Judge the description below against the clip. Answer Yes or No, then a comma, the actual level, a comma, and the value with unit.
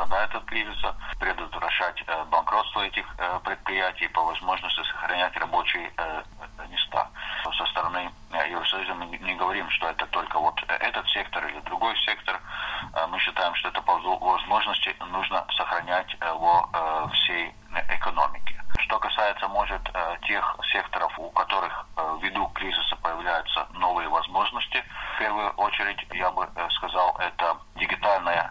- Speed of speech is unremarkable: Yes, average, 120 wpm